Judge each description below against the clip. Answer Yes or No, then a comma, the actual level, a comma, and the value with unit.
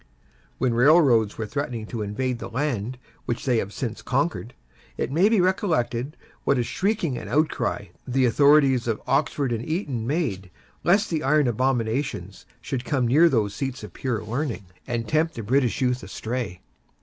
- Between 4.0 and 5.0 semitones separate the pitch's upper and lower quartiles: Yes, average, 4.3 semitones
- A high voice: No, low, 125 Hz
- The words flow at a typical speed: Yes, average, 165 wpm